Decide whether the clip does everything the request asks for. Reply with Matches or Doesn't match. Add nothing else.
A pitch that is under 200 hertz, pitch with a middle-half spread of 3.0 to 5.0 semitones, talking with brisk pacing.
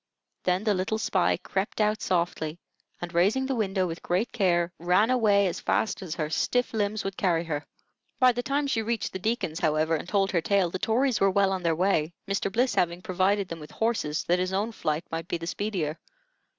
Matches